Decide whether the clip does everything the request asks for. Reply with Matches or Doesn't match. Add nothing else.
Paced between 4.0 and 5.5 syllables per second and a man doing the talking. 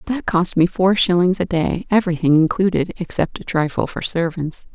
Doesn't match